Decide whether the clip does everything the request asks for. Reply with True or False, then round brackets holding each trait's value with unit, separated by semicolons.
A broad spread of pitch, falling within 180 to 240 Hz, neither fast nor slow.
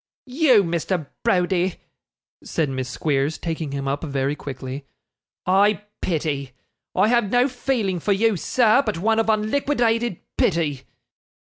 False (7.4 semitones; 185 Hz; 130 wpm)